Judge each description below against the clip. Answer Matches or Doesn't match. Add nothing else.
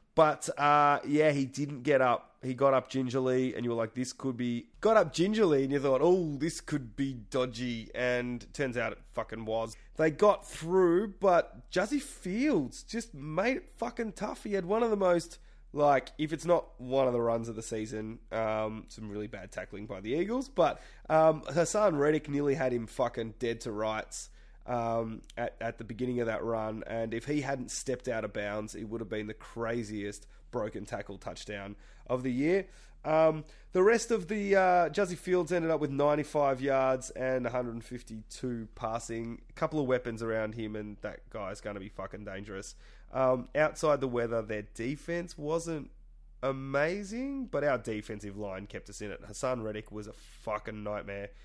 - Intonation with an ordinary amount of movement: Doesn't match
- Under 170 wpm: Doesn't match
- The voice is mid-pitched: Doesn't match